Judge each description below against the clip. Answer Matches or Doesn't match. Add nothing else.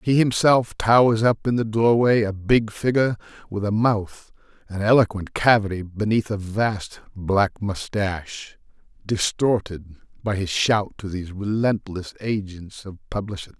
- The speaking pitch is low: Matches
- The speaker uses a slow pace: Matches